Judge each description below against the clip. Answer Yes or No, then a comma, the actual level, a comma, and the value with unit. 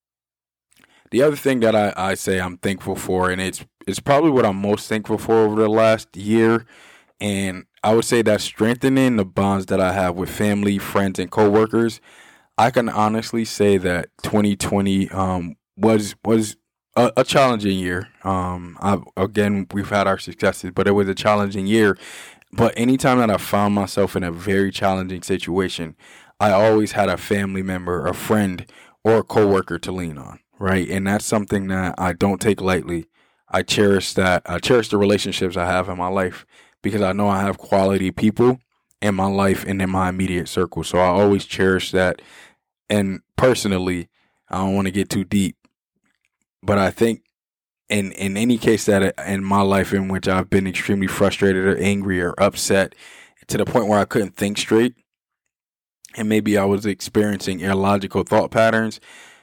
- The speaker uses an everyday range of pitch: No, narrow, 2.3 semitones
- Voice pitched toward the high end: No, low, 100 Hz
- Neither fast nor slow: Yes, average, 180 wpm